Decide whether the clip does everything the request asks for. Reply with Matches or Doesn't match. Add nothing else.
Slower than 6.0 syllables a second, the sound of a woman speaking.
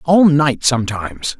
Doesn't match